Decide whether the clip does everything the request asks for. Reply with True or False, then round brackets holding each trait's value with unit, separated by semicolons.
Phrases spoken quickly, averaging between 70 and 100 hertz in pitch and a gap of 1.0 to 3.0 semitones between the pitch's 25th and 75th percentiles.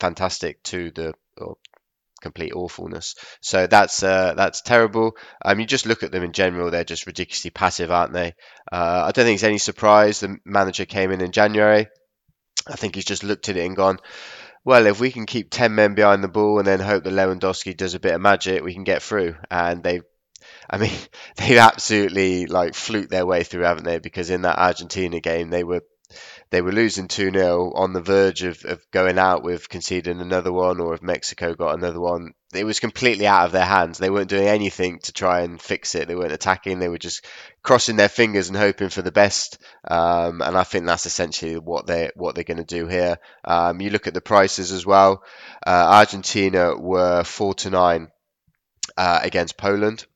True (210 wpm; 95 Hz; 2.5 semitones)